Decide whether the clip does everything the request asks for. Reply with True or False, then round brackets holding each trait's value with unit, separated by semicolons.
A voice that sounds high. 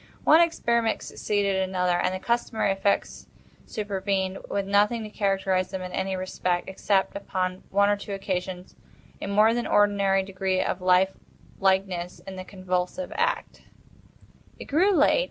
True (195 Hz)